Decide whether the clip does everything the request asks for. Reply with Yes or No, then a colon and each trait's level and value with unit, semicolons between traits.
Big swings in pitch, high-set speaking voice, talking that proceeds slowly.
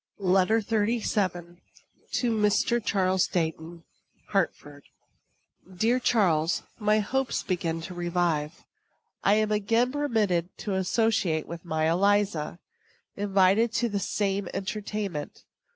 No: average, 3.7 semitones; high, 195 Hz; slow, 105 wpm